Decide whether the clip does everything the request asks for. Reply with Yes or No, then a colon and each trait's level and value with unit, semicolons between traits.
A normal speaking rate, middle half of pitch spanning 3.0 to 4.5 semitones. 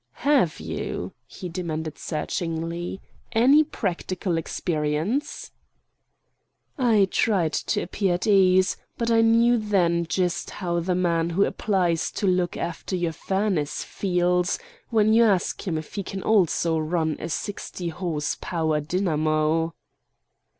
No: slow, 130 wpm; average, 3.5 semitones